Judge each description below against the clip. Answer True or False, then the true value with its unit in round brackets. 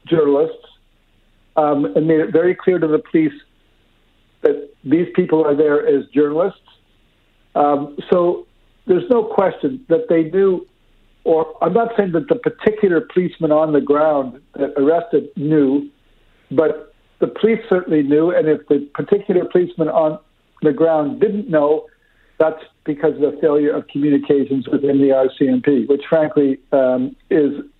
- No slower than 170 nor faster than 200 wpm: False (145 wpm)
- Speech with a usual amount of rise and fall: True (4.0 semitones)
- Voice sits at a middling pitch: True (155 Hz)